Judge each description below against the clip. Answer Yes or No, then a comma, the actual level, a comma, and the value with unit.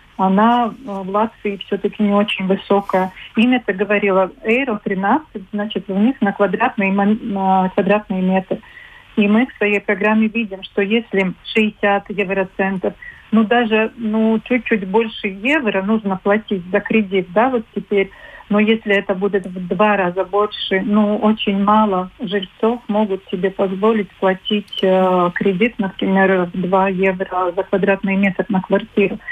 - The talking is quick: No, average, 140 wpm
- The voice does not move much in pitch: Yes, narrow, 2.2 semitones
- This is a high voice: Yes, high, 205 Hz